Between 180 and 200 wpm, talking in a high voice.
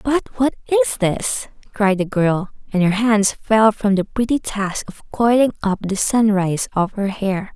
Yes: average, 185 wpm; high, 205 Hz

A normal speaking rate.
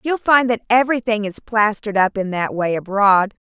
Yes: average, 190 wpm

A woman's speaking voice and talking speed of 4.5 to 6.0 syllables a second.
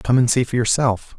No: male; 5.2 syllables/s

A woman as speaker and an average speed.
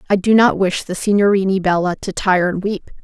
No: female; fast, 220 wpm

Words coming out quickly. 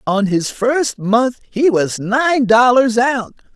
No: average, 150 wpm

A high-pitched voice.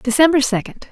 Yes: very high, 270 Hz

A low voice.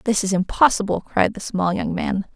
No: high, 200 Hz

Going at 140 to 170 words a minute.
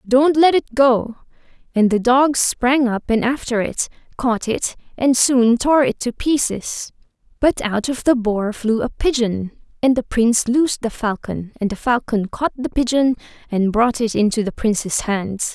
No: average, 180 wpm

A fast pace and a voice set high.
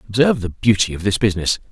No: fast, 210 wpm; low, 105 Hz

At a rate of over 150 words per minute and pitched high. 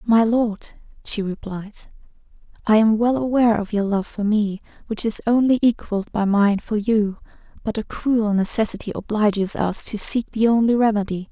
Yes: average, 170 wpm; high, 215 Hz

